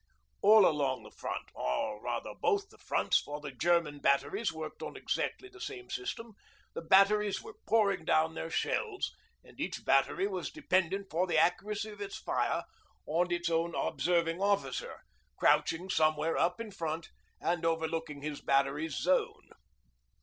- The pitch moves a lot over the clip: No, average, 4.6 semitones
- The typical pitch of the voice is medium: Yes, medium, 170 Hz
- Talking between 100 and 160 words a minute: Yes, average, 155 wpm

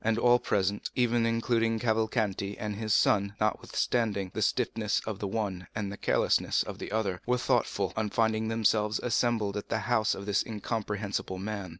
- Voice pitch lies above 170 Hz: No, low, 110 Hz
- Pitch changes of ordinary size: No, narrow, 2.0 semitones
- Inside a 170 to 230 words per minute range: Yes, average, 175 wpm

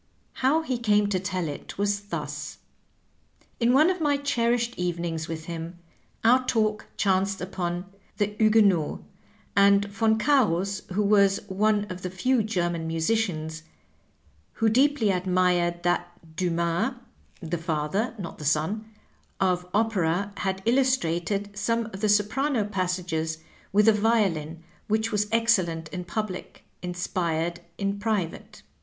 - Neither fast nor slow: No, slow, 130 wpm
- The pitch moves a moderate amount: Yes, average, 4.1 semitones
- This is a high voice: Yes, high, 200 Hz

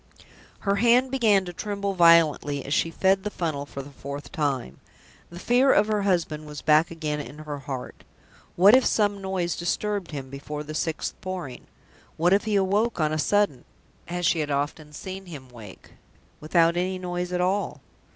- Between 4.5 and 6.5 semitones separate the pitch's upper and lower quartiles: Yes, average, 4.9 semitones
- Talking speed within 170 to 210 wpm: Yes, average, 180 wpm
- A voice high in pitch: No, medium, 170 Hz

